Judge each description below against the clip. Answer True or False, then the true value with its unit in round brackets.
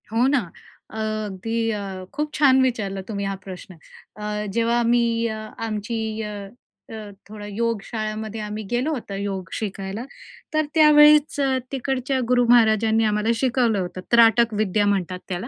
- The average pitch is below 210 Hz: False (220 Hz)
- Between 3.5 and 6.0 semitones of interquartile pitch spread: False (2.9 semitones)